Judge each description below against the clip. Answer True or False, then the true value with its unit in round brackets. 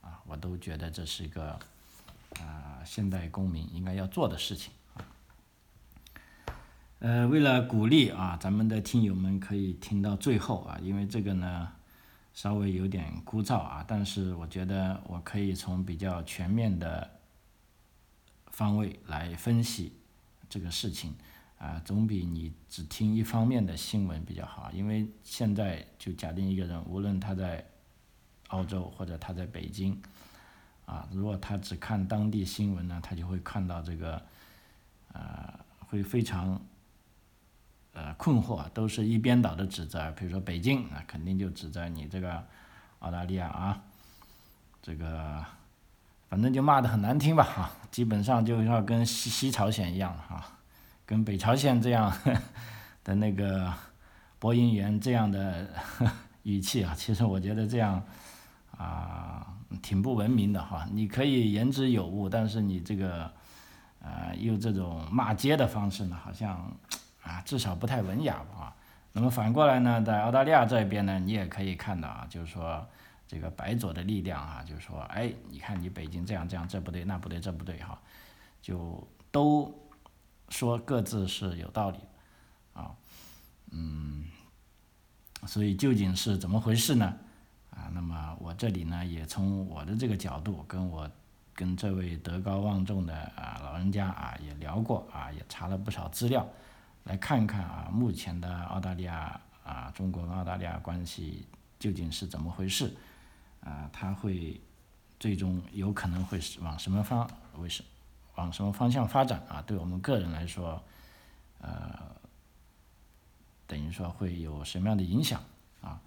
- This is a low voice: True (95 Hz)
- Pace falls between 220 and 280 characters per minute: True (230 characters per minute)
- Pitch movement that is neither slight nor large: True (3.8 semitones)